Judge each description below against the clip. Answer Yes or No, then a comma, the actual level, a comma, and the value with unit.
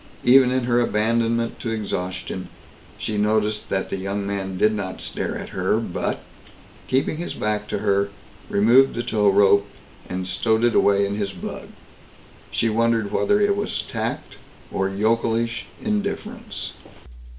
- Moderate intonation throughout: Yes, average, 3.1 semitones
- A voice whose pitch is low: Yes, low, 110 Hz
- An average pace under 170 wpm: Yes, average, 150 wpm